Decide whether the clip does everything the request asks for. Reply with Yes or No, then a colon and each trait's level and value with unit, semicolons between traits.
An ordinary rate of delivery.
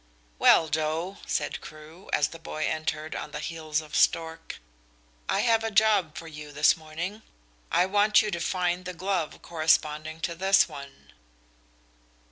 Yes: average, 155 wpm